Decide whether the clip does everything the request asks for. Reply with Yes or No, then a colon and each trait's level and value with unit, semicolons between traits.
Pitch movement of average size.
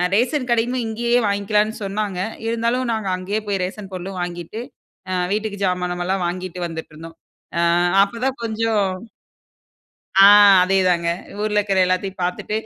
Yes: average, 3.2 semitones